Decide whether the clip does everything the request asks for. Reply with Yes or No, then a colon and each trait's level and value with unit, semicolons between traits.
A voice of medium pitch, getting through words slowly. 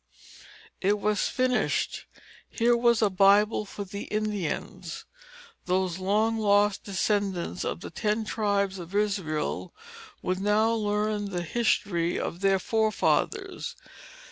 No: high, 205 Hz; slow, 115 wpm